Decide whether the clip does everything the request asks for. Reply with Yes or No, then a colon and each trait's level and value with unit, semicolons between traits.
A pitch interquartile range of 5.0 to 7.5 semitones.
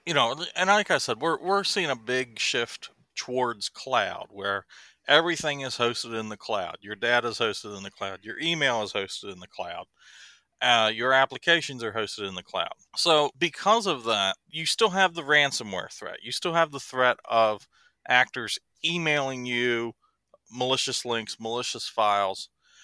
Yes: wide, 5.4 semitones